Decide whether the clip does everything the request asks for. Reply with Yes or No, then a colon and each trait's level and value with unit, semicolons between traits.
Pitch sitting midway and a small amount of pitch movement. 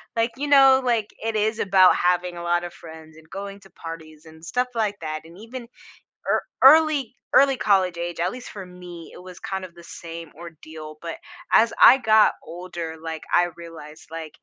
No: medium, 180 Hz; average, 4.9 semitones